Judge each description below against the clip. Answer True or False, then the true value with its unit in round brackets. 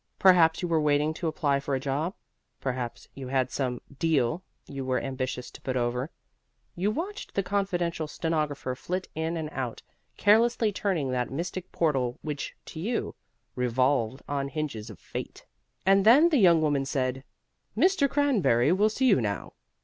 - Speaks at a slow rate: False (165 wpm)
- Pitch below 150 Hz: False (155 Hz)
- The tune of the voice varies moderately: False (6.2 semitones)